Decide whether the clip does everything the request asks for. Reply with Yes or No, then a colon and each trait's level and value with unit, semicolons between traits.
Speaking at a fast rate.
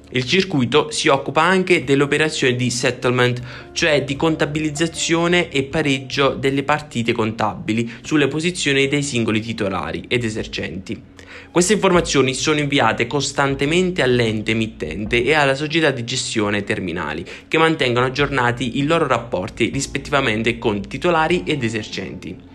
No: average, 125 wpm